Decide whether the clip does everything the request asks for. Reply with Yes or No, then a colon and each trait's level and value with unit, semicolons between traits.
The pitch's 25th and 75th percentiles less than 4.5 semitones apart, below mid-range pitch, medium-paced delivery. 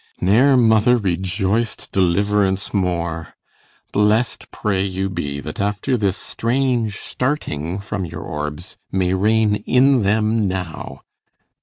No: average, 3.5 semitones; low, 100 Hz; slow, 120 wpm